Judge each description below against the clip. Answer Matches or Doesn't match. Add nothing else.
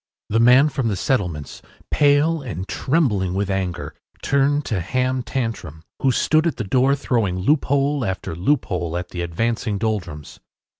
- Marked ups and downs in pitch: Matches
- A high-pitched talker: Doesn't match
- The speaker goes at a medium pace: Matches